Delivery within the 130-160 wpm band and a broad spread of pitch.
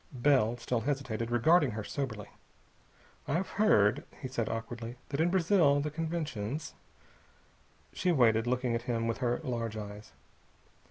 No: average, 140 wpm; average, 4.6 semitones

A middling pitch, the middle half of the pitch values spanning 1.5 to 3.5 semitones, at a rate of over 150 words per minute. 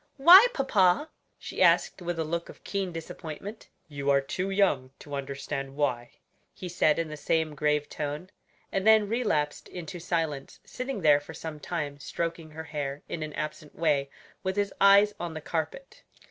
No: medium, 160 Hz; average, 4.3 semitones; average, 175 wpm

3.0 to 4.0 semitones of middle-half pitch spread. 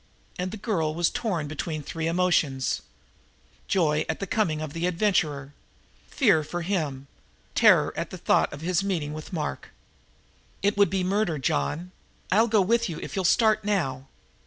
No: average, 4.5 semitones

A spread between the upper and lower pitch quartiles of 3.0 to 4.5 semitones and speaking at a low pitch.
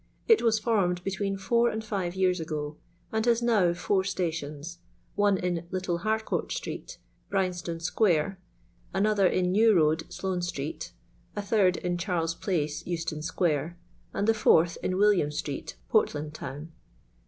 No: average, 3.7 semitones; medium, 180 Hz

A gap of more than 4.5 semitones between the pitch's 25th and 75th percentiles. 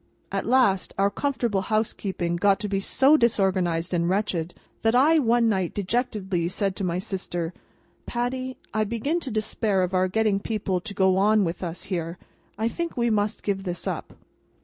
No: average, 3.8 semitones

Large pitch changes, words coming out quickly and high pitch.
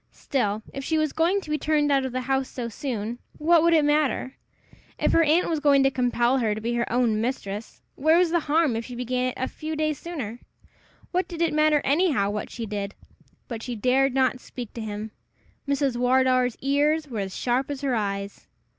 No: average, 4.3 semitones; fast, 215 wpm; very high, 260 Hz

